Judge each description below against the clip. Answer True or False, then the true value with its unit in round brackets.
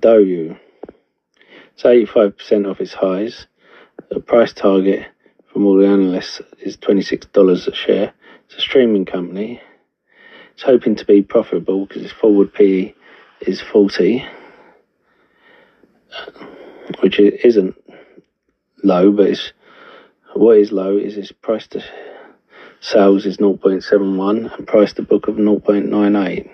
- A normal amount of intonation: False (1.3 semitones)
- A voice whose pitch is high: False (100 Hz)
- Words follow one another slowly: True (120 wpm)